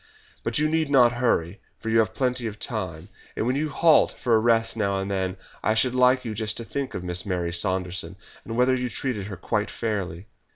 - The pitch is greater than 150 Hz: No, low, 110 Hz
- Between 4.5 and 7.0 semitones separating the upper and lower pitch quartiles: Yes, average, 4.9 semitones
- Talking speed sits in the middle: No, fast, 220 wpm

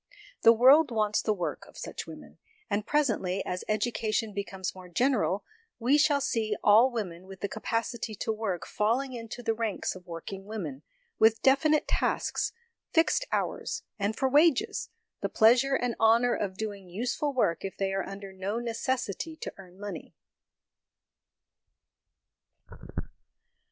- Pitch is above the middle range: Yes, high, 220 Hz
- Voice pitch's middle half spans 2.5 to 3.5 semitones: No, average, 4.1 semitones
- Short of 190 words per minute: Yes, average, 145 wpm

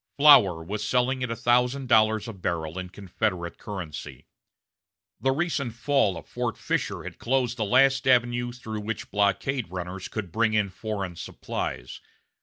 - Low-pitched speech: Yes, low, 110 Hz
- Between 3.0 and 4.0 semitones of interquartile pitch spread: No, average, 4.7 semitones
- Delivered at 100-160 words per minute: Yes, average, 155 wpm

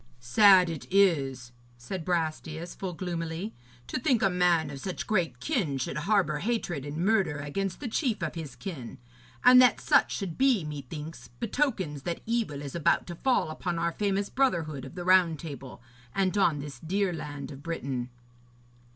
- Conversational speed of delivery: Yes, average, 170 wpm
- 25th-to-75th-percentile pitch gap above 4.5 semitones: Yes, average, 5.0 semitones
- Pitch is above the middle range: No, medium, 170 Hz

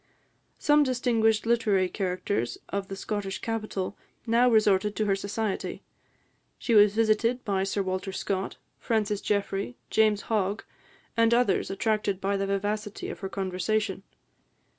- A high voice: Yes, high, 205 Hz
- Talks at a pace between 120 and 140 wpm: Yes, slow, 135 wpm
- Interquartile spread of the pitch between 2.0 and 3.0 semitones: Yes, narrow, 2.4 semitones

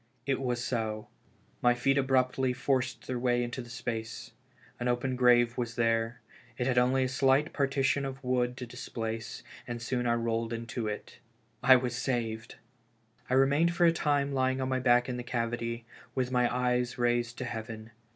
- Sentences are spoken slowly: No, average, 175 wpm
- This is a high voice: No, low, 125 Hz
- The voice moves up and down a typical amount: No, narrow, 1.8 semitones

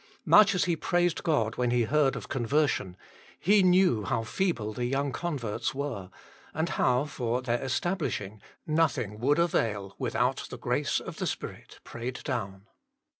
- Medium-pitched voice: No, low, 130 Hz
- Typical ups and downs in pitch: No, wide, 6.1 semitones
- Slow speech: No, average, 160 wpm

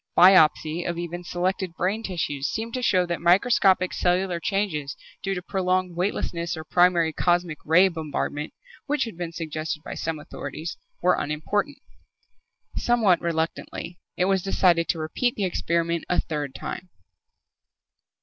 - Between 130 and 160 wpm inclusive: Yes, average, 140 wpm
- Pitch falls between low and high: Yes, medium, 175 Hz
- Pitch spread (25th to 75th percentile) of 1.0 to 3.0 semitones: Yes, narrow, 2.5 semitones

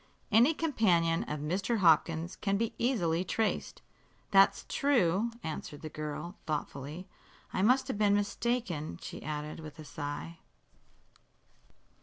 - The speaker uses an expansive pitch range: Yes, wide, 6.1 semitones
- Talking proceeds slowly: Yes, slow, 125 wpm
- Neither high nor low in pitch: Yes, medium, 175 Hz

